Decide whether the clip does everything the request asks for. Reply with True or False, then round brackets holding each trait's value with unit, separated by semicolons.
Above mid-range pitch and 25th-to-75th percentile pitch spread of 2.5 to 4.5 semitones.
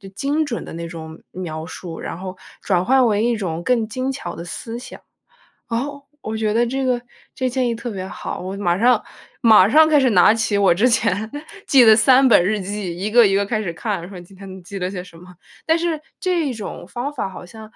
False (215 Hz; 5.1 semitones)